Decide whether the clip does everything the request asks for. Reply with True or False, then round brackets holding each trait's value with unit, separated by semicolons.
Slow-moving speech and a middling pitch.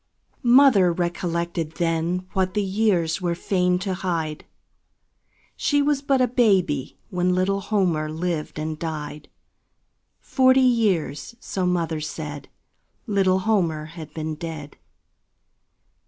True (115 wpm; 180 Hz)